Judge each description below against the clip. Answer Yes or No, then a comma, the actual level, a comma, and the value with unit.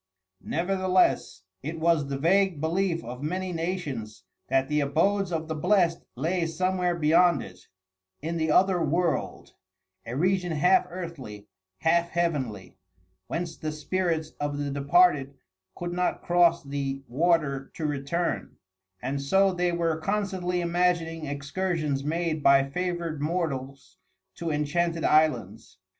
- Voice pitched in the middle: Yes, medium, 165 Hz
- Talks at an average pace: No, slow, 130 wpm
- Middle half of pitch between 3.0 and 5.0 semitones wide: Yes, average, 3.7 semitones